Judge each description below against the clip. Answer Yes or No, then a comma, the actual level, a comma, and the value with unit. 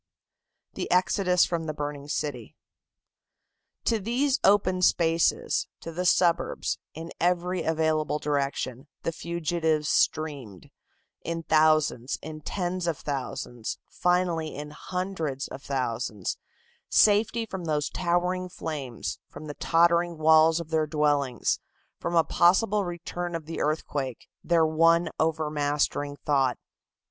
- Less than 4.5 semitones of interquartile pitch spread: Yes, average, 3.0 semitones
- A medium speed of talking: No, slow, 120 wpm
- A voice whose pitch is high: No, medium, 160 Hz